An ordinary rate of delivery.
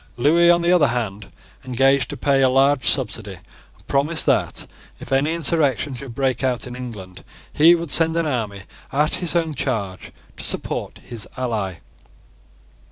Yes: average, 165 wpm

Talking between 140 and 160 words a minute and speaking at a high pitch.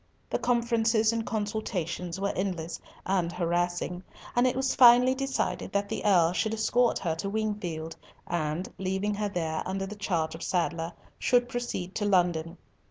Yes: average, 155 wpm; high, 195 Hz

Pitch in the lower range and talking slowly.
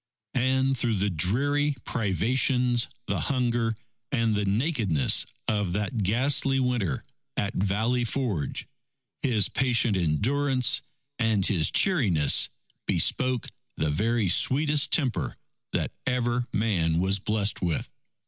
Yes: low, 115 Hz; slow, 110 wpm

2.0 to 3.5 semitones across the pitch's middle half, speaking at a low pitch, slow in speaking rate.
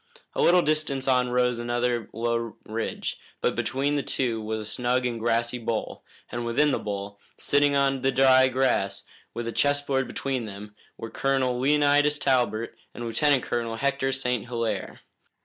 No: average, 2.8 semitones; low, 125 Hz; average, 165 wpm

